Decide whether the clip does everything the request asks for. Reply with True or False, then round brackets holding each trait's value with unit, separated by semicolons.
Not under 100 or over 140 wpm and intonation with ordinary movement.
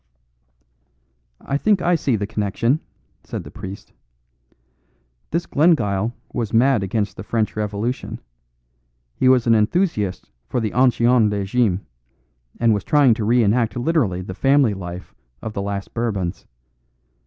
True (135 wpm; 4.0 semitones)